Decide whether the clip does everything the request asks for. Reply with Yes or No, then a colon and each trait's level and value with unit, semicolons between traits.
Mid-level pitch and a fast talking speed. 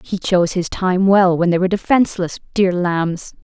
No: medium, 180 Hz; average, 190 wpm